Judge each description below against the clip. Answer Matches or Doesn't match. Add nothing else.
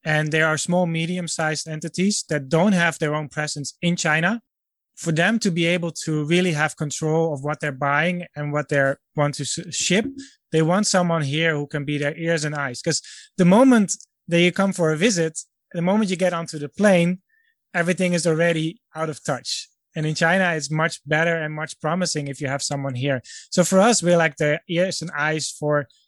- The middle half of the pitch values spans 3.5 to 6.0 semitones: Doesn't match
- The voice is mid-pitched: Matches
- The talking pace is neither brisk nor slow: Doesn't match